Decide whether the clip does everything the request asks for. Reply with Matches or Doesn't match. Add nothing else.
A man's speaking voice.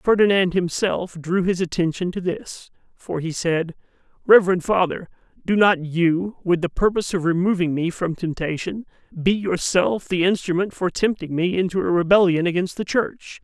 Matches